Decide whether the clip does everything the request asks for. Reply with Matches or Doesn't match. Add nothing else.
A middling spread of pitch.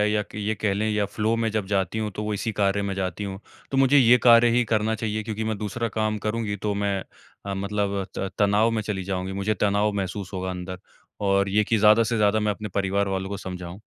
Doesn't match